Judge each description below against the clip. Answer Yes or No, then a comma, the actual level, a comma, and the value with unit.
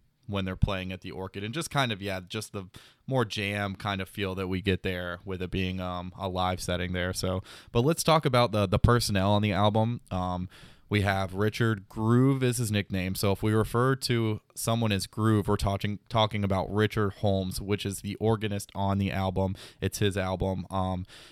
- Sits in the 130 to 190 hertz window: No, low, 100 Hz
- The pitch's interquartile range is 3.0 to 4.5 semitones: No, narrow, 2.6 semitones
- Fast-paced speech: Yes, fast, 210 wpm